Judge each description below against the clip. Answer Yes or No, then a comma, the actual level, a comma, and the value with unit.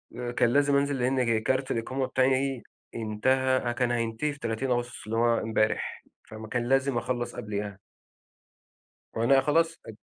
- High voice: No, low, 120 Hz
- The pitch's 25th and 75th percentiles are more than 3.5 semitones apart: No, average, 2.9 semitones